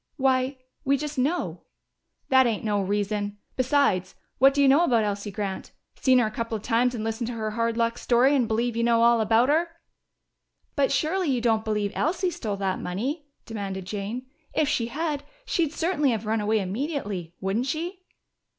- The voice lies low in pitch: No, high, 235 Hz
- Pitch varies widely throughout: No, average, 4.8 semitones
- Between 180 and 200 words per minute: Yes, average, 185 wpm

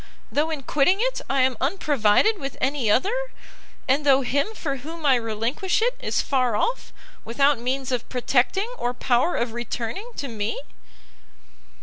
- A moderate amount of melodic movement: Yes, average, 4.5 semitones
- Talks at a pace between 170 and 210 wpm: No, average, 155 wpm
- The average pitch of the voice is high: Yes, very high, 270 Hz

